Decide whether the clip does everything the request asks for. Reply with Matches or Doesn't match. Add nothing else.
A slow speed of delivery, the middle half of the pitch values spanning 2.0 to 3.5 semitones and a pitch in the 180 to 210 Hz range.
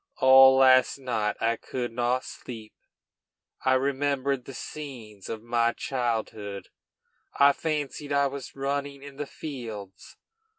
Doesn't match